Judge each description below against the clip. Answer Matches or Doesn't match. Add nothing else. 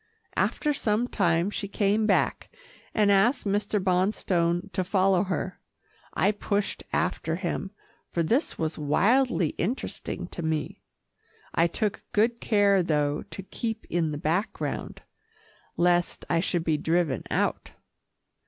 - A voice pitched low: Doesn't match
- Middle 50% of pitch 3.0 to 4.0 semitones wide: Matches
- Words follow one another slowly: Matches